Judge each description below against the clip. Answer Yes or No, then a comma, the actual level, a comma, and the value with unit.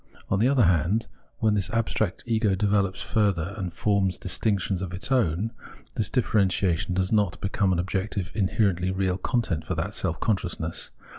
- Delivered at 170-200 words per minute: No, average, 160 wpm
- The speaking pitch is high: No, very low, 95 Hz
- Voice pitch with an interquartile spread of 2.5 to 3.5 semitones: Yes, average, 2.8 semitones